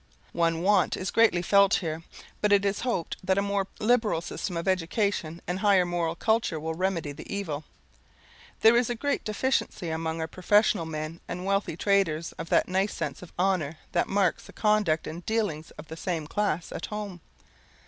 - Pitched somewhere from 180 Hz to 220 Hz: Yes, medium, 185 Hz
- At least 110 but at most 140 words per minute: No, average, 190 wpm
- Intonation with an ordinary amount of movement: Yes, average, 3.7 semitones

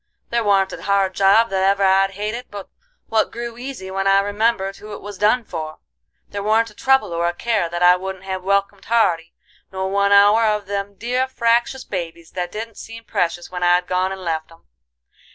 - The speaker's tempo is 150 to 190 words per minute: No, fast, 205 wpm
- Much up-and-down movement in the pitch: No, average, 3.0 semitones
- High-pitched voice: Yes, high, 200 Hz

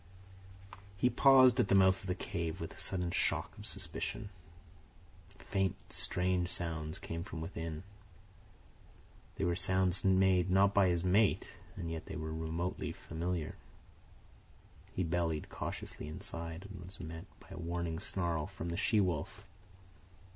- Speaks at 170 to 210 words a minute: No, average, 145 wpm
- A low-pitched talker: Yes, very low, 90 Hz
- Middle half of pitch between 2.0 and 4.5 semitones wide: Yes, narrow, 2.6 semitones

